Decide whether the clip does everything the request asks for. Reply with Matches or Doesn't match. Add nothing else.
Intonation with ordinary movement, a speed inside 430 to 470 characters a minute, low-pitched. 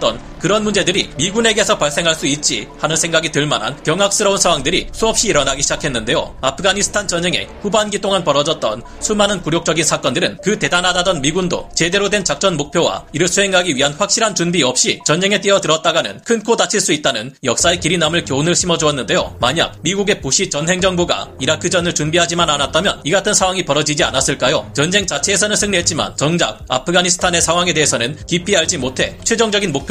Doesn't match